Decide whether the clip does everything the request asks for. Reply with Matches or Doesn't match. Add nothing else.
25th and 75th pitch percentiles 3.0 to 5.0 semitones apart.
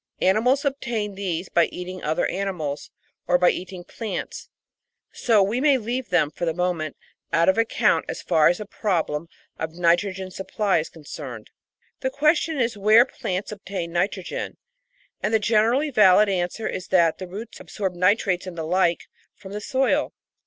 Matches